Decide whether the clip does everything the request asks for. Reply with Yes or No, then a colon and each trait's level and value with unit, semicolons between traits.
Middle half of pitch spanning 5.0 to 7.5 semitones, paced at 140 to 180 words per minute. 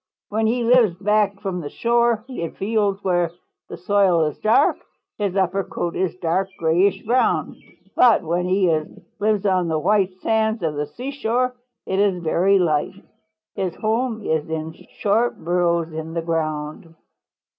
No: average, 4.3 semitones; average, 155 wpm